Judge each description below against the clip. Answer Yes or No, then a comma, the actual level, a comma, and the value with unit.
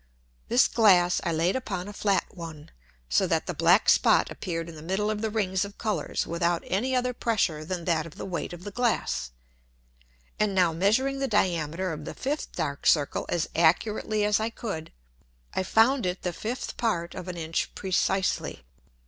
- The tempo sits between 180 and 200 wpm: Yes, average, 185 wpm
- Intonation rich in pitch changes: No, average, 4.3 semitones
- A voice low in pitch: No, medium, 185 Hz